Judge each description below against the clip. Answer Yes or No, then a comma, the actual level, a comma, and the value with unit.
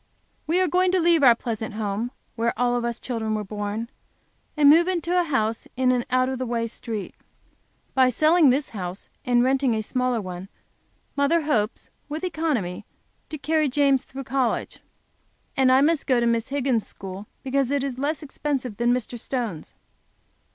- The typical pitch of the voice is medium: No, very high, 255 Hz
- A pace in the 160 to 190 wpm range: Yes, average, 175 wpm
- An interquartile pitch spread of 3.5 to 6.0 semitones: Yes, average, 4.0 semitones